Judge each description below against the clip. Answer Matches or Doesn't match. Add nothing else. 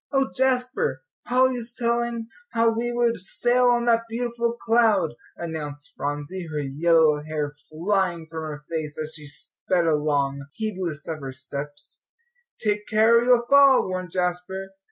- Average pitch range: Doesn't match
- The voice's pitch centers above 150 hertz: Matches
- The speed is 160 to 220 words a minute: Doesn't match